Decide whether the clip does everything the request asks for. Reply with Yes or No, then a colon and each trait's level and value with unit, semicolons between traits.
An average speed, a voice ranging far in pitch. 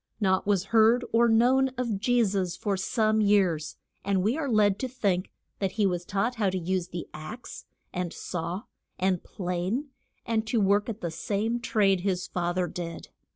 No: average, 185 wpm; average, 3.6 semitones